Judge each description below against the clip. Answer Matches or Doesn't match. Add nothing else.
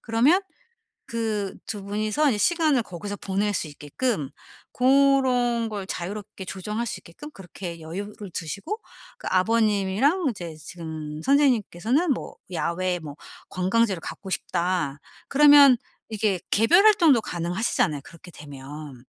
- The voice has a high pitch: Matches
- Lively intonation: Matches